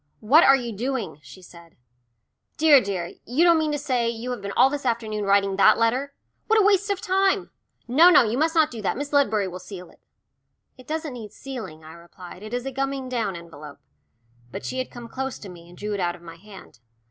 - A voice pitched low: No, high, 235 Hz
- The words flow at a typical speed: No, fast, 230 wpm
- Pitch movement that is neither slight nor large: No, wide, 6.3 semitones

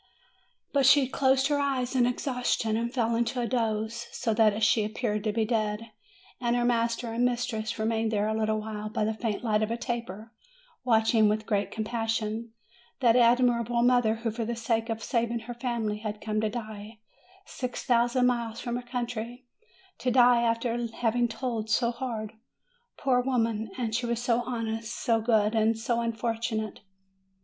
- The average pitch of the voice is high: Yes, high, 230 Hz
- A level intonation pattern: Yes, narrow, 1.8 semitones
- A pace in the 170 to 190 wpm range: Yes, average, 175 wpm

